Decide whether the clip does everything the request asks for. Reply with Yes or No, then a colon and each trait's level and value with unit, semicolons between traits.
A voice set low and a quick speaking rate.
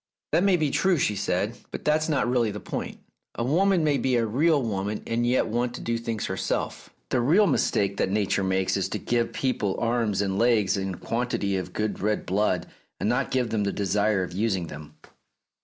Yes: low, 115 Hz; fast, 210 wpm